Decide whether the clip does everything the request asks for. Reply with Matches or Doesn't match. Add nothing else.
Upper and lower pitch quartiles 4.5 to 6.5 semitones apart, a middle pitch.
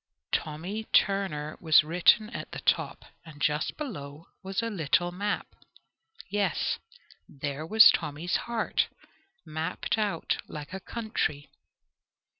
Matches